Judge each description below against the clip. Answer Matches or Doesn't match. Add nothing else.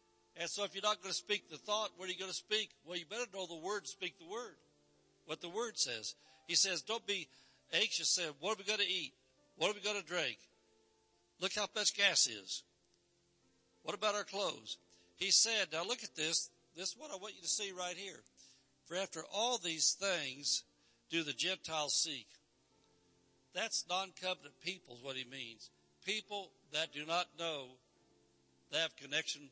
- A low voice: Doesn't match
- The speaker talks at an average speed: Matches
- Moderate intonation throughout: Doesn't match